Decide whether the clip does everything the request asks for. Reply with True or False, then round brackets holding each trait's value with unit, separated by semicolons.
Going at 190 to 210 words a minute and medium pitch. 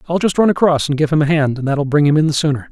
False (355 wpm; 150 Hz)